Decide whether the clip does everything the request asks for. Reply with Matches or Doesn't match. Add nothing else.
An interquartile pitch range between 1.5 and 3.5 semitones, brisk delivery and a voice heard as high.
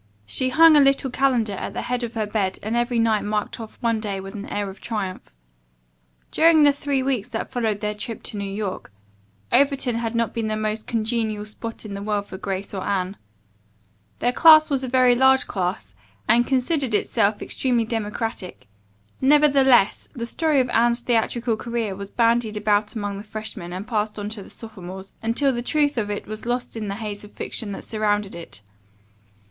Doesn't match